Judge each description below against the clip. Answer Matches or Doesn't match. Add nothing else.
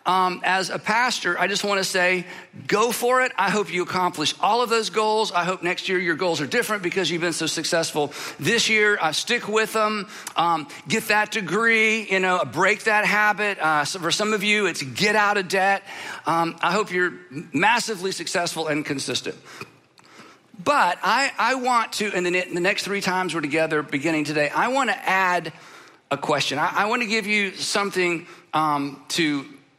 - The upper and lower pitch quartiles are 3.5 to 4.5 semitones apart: Matches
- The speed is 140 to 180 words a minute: Doesn't match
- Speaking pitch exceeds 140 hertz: Matches